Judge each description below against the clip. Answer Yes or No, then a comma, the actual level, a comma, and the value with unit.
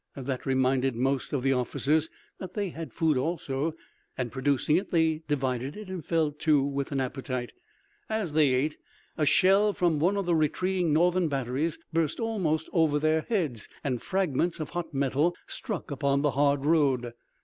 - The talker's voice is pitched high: No, medium, 150 Hz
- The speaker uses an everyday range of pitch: Yes, average, 3.9 semitones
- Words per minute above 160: Yes, average, 170 wpm